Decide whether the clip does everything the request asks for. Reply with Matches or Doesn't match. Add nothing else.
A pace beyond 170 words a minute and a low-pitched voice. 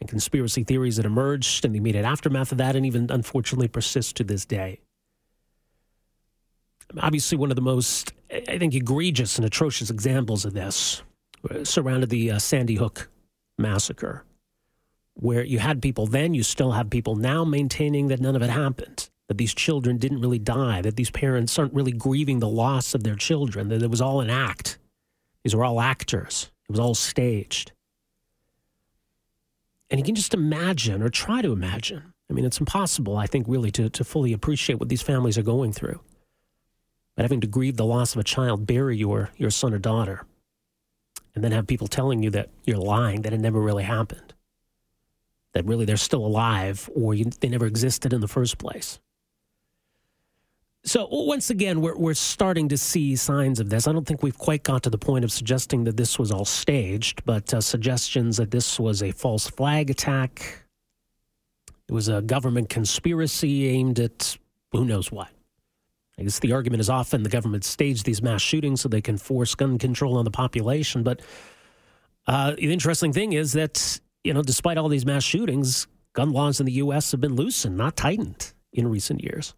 Matches